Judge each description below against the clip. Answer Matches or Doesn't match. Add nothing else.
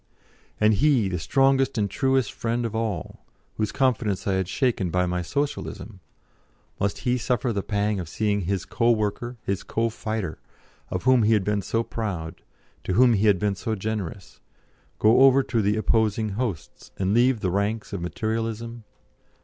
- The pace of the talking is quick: Doesn't match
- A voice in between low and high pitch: Doesn't match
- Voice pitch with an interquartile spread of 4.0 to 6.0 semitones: Doesn't match